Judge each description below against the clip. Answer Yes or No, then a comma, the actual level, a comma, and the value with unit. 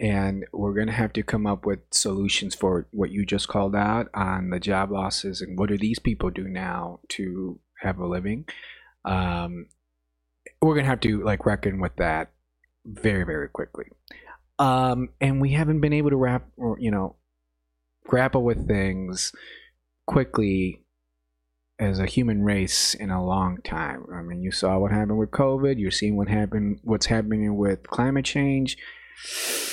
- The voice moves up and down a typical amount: Yes, average, 3.9 semitones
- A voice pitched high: No, low, 100 Hz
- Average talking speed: Yes, average, 170 wpm